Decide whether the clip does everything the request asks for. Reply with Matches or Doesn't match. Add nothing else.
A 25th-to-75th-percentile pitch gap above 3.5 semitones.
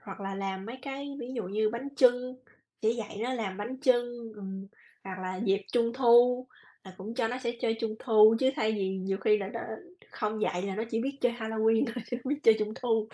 Doesn't match